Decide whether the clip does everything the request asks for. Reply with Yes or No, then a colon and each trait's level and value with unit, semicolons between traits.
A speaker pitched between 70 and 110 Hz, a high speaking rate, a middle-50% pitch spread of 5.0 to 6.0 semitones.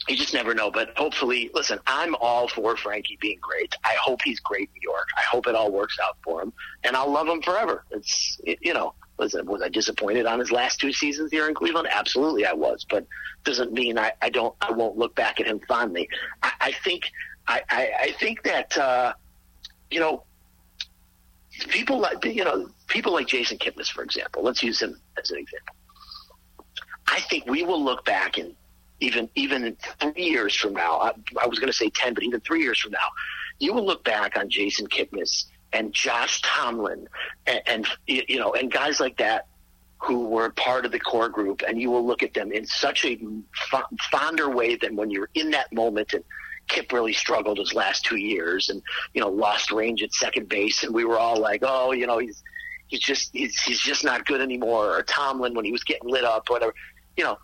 No: low, 120 Hz; fast, 210 wpm; wide, 5.4 semitones